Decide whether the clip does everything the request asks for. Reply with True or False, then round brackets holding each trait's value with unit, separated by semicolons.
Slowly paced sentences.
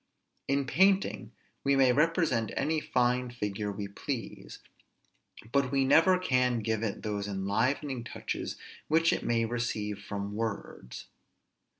True (125 wpm)